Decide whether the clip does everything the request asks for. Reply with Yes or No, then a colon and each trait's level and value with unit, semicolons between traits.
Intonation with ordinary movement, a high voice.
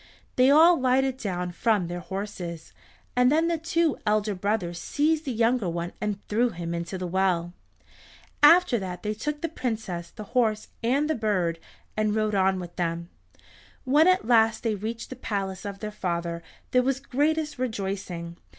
No: wide, 6.0 semitones; high, 215 Hz